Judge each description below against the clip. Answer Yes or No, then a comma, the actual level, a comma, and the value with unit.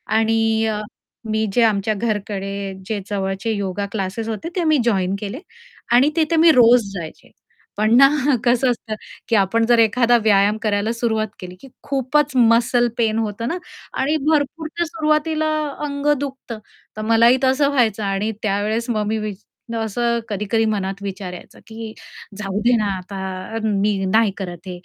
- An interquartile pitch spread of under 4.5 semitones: Yes, average, 3.2 semitones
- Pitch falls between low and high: No, high, 220 Hz